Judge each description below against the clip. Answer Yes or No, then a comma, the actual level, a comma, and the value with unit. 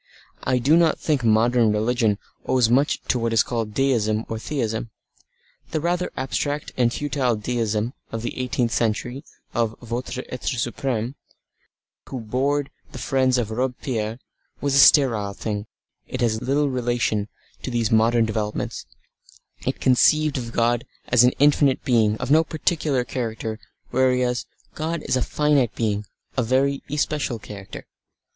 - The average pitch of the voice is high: No, low, 125 Hz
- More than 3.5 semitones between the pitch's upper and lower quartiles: No, average, 3.2 semitones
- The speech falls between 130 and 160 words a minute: Yes, average, 150 wpm